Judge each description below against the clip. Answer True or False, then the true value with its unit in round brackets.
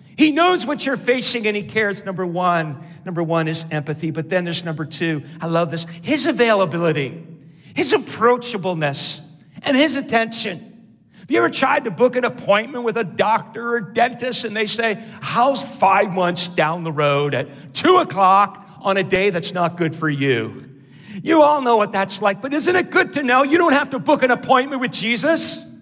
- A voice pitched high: True (205 Hz)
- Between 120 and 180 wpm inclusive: False (195 wpm)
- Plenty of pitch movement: True (7.1 semitones)